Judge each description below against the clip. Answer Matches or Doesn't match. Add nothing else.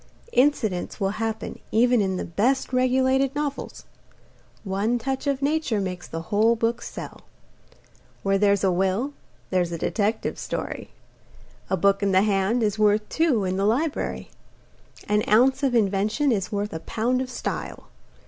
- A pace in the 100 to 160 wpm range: Matches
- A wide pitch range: Doesn't match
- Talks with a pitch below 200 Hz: Doesn't match